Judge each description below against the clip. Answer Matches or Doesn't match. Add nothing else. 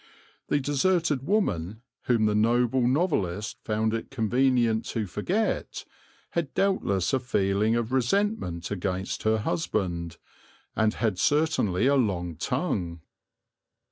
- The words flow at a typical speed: Doesn't match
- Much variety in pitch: Matches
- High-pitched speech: Doesn't match